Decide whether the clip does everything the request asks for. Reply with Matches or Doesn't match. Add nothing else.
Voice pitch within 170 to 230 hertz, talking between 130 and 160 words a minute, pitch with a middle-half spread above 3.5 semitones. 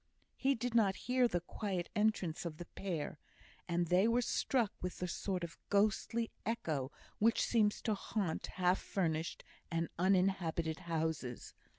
Matches